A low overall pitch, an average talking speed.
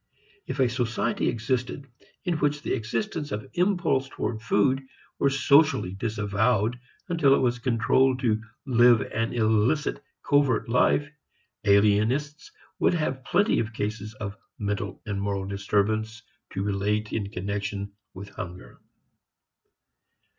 No: low, 115 Hz; slow, 125 wpm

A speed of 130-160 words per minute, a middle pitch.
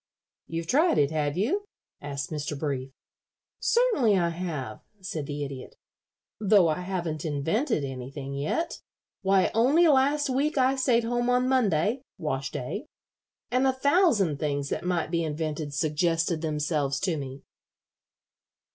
Yes: average, 140 wpm; medium, 170 Hz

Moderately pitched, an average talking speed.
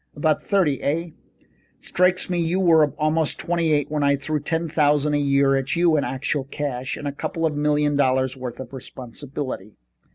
Yes: medium, 145 Hz; average, 185 wpm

